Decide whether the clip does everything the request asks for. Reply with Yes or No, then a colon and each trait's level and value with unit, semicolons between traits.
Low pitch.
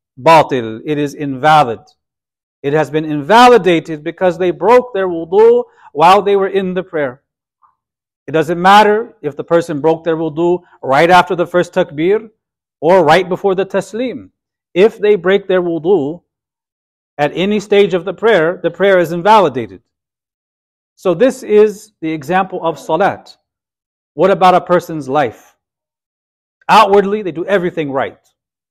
No: medium, 175 Hz